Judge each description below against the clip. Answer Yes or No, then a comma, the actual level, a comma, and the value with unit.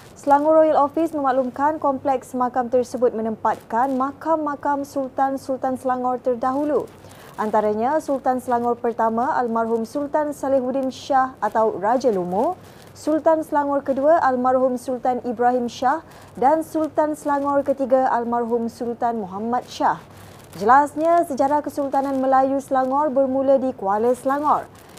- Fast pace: No, average, 115 wpm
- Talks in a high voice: Yes, very high, 265 Hz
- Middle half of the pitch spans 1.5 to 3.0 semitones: Yes, narrow, 2.6 semitones